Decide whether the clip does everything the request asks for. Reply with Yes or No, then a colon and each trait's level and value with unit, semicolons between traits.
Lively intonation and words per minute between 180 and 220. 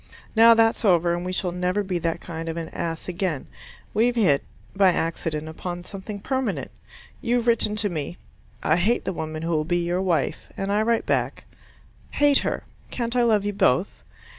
No: average, 4.5 semitones; average, 190 wpm